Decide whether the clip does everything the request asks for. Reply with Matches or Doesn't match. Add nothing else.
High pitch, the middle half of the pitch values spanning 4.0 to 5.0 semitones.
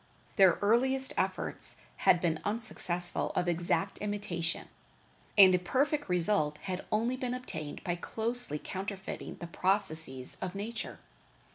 Matches